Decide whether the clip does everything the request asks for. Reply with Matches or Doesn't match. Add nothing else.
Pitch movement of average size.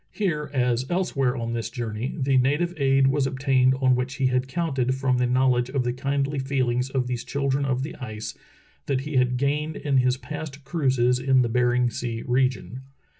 Doesn't match